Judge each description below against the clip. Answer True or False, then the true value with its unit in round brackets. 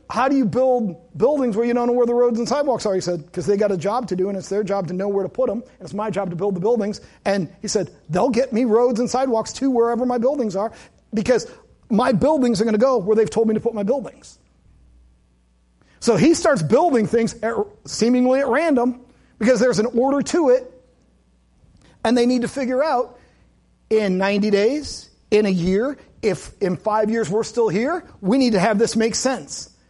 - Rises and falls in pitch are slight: False (4.0 semitones)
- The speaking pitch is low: False (225 Hz)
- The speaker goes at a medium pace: False (225 wpm)